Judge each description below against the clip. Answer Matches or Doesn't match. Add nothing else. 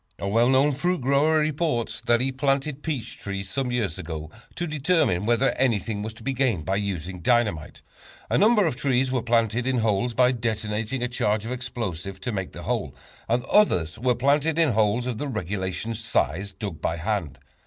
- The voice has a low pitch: Matches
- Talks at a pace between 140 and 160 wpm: Doesn't match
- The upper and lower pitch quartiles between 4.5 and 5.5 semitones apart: Matches